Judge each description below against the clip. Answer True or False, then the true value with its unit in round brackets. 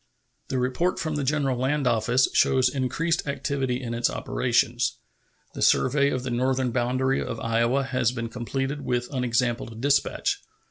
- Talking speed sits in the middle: True (150 wpm)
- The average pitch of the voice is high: False (130 Hz)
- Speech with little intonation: True (2.1 semitones)